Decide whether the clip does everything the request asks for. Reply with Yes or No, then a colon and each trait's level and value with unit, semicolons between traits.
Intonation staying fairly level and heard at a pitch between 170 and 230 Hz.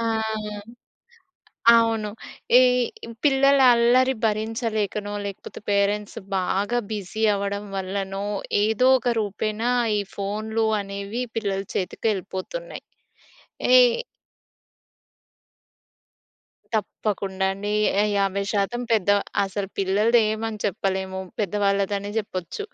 Yes: narrow, 2.1 semitones; high, 205 Hz